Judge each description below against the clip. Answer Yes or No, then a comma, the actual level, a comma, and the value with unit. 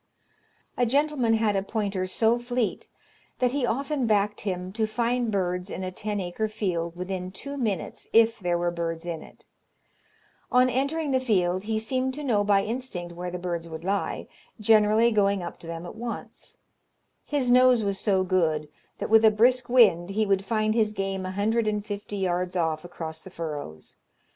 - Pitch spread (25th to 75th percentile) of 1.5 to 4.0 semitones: No, average, 4.5 semitones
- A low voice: No, high, 205 Hz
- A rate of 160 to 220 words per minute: Yes, average, 185 wpm